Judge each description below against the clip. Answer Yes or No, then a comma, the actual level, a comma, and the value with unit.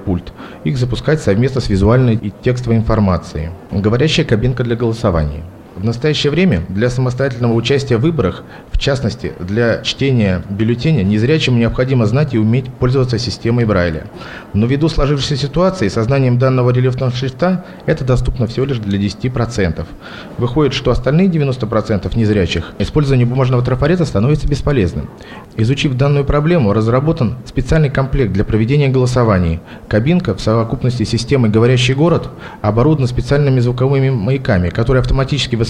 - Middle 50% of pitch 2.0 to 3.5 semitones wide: No, average, 4.0 semitones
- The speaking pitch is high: No, low, 125 Hz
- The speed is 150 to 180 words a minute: No, average, 135 wpm